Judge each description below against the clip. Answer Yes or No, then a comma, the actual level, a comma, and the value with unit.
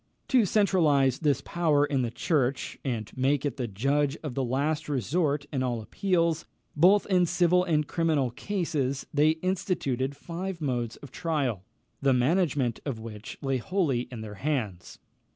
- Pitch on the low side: No, medium, 145 Hz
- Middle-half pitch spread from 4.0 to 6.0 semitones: Yes, average, 4.7 semitones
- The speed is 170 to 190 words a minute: No, average, 155 wpm